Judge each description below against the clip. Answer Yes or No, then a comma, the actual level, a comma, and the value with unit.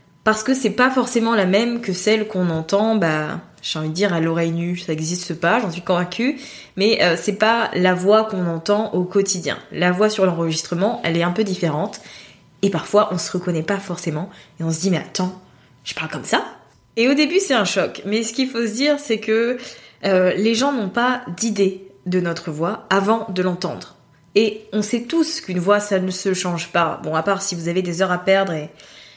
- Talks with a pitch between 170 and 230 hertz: Yes, high, 190 Hz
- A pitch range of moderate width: Yes, average, 4.2 semitones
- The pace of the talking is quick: Yes, fast, 225 wpm